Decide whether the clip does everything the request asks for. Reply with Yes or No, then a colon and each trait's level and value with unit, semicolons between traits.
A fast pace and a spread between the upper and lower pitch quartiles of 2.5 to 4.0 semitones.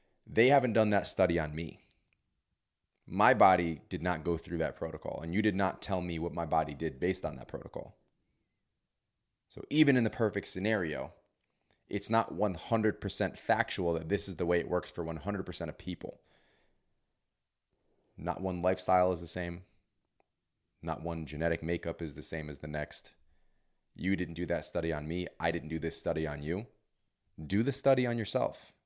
No: average, 175 wpm; average, 3.5 semitones